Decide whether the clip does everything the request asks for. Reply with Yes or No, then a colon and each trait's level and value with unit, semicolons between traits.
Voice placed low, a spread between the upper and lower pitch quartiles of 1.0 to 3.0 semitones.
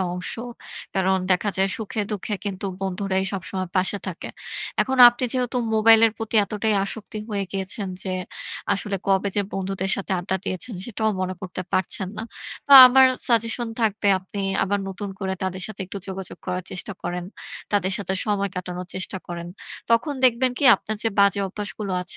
No: high, 200 Hz; narrow, 2.6 semitones